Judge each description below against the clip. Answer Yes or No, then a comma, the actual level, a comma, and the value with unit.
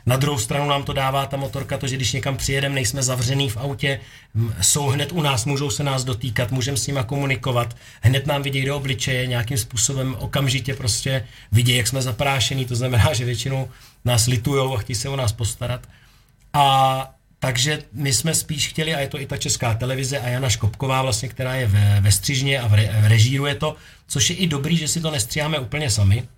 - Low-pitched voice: Yes, low, 130 Hz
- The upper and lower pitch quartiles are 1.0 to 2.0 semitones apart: No, narrow, 2.4 semitones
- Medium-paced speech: No, fast, 210 wpm